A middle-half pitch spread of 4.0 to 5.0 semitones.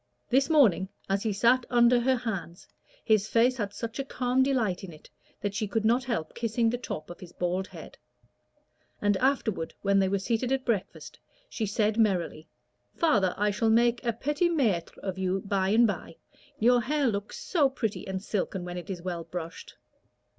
Yes: average, 4.3 semitones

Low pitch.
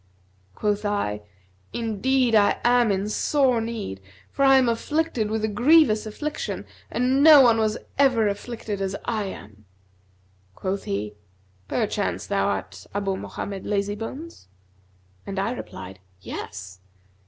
No: high, 215 Hz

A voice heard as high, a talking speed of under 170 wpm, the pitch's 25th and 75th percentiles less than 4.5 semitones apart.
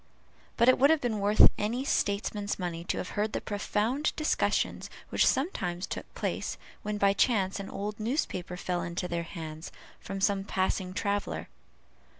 Yes: high, 200 Hz; average, 160 wpm; average, 3.0 semitones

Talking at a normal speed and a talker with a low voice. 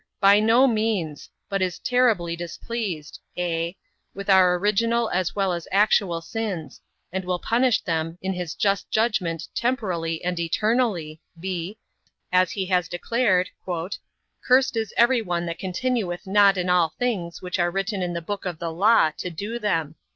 No: average, 165 wpm; medium, 185 Hz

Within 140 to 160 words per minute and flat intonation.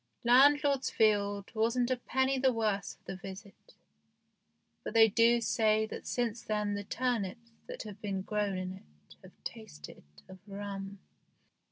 No: average, 150 wpm; average, 3.3 semitones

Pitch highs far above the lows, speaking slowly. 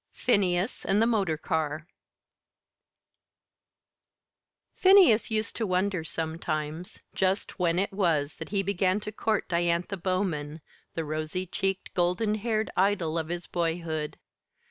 No: average, 3.8 semitones; slow, 120 wpm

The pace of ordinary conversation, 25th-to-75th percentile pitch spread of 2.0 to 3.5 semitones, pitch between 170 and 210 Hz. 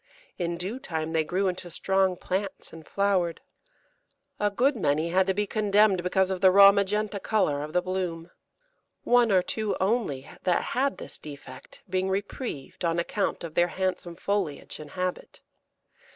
Yes: average, 165 wpm; average, 3.0 semitones; medium, 185 Hz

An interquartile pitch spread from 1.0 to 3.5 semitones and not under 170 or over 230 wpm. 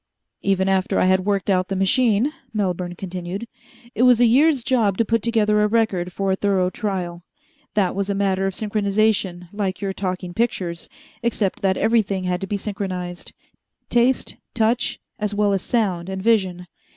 Yes: average, 2.9 semitones; average, 175 wpm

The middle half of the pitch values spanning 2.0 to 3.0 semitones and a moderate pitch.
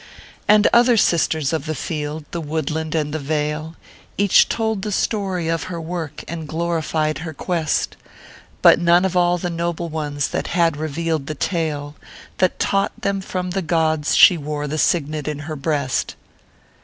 Yes: narrow, 2.5 semitones; medium, 160 Hz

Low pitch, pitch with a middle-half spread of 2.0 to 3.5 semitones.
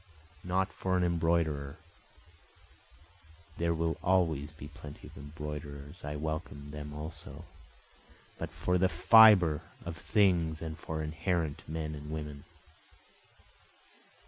Yes: very low, 80 Hz; narrow, 2.6 semitones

